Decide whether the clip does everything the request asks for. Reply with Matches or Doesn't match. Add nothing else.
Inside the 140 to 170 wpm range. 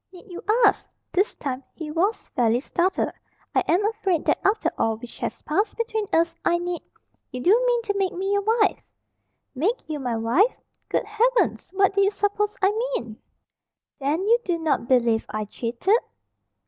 Doesn't match